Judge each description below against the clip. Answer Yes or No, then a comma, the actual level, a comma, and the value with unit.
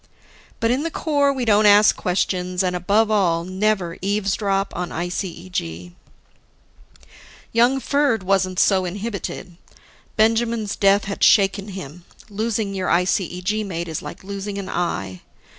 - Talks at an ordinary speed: No, slow, 130 wpm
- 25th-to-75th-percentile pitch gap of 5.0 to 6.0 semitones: No, average, 3.1 semitones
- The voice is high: Yes, high, 195 Hz